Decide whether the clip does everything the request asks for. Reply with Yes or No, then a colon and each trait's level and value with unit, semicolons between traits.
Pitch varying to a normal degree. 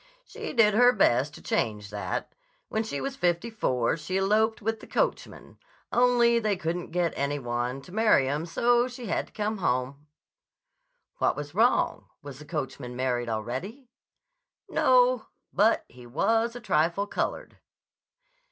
No: wide, 9.0 semitones